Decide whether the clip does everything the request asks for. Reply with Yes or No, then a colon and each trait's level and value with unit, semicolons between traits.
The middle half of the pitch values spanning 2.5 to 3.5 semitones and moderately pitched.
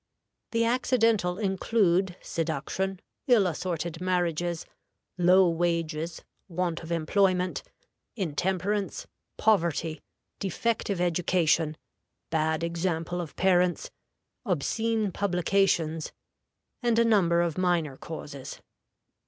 Yes: average, 2.8 semitones; medium, 180 Hz